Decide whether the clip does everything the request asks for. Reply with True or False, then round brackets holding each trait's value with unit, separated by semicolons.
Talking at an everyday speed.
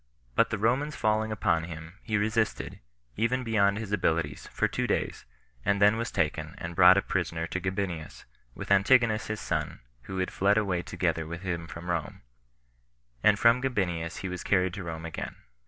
True (180 wpm)